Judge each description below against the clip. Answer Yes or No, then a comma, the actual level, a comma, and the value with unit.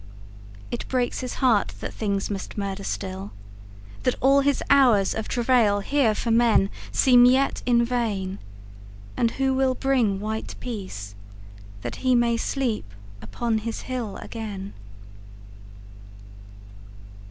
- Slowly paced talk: Yes, slow, 115 wpm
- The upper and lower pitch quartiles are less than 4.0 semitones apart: No, average, 4.8 semitones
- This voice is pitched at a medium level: No, high, 220 Hz